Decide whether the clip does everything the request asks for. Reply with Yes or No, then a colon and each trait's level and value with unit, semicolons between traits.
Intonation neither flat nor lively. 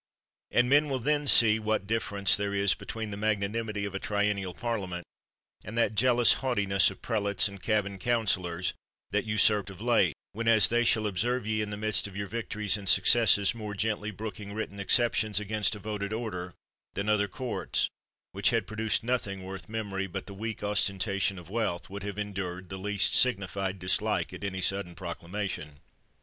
No: narrow, 2.3 semitones